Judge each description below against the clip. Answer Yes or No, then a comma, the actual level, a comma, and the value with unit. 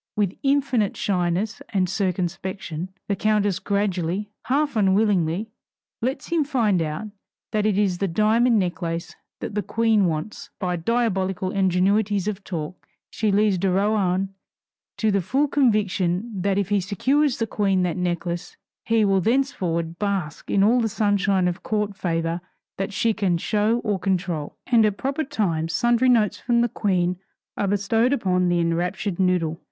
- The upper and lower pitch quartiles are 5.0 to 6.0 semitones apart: No, average, 3.3 semitones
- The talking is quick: No, average, 155 wpm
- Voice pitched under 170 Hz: No, high, 200 Hz